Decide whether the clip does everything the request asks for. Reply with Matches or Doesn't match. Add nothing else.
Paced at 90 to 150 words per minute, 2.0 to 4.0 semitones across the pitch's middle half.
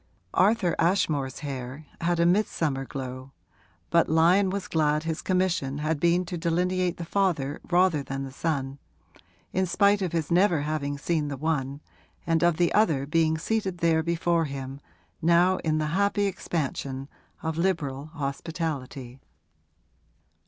Matches